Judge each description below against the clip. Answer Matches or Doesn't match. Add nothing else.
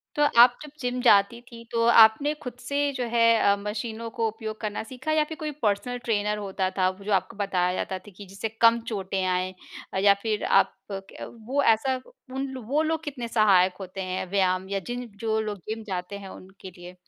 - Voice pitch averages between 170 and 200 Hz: Doesn't match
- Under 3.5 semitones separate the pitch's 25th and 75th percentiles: Doesn't match